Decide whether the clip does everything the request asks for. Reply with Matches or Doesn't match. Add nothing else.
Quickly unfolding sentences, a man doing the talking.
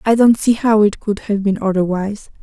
Doesn't match